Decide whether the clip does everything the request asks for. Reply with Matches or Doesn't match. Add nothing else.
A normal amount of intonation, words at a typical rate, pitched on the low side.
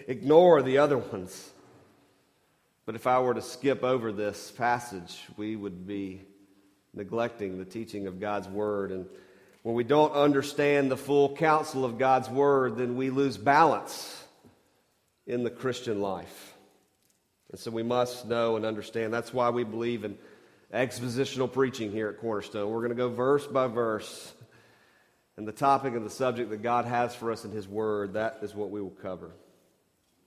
Matches